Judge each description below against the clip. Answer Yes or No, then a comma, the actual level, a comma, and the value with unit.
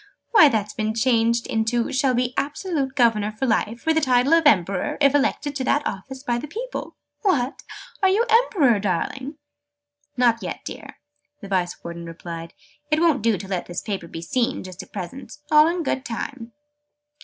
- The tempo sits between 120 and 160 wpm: No, average, 180 wpm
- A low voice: No, high, 245 Hz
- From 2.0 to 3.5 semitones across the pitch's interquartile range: No, wide, 5.6 semitones